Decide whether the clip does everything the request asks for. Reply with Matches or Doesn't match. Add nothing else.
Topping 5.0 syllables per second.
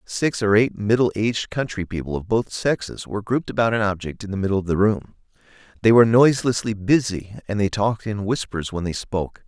Matches